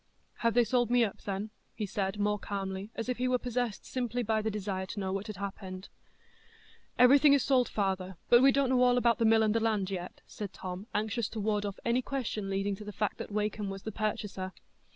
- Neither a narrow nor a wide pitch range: Yes, average, 3.5 semitones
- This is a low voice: No, high, 215 Hz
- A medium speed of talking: No, fast, 230 wpm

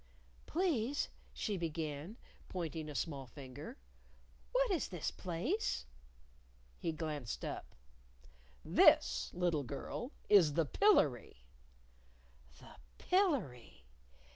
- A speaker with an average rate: No, slow, 90 wpm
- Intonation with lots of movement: Yes, wide, 9.0 semitones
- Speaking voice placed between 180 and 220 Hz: No, medium, 165 Hz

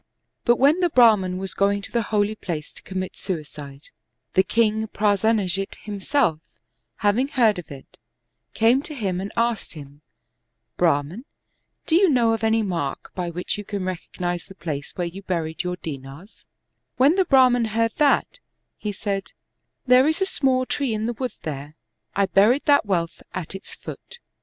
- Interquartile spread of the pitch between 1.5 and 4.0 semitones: No, average, 5.2 semitones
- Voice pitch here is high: Yes, high, 205 Hz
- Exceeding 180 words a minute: No, average, 175 wpm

